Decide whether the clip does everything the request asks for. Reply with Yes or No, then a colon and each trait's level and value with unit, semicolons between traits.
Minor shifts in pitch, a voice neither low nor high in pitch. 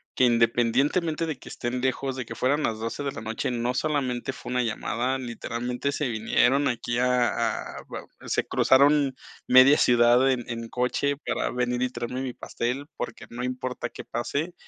No: narrow, 2.2 semitones; low, 125 Hz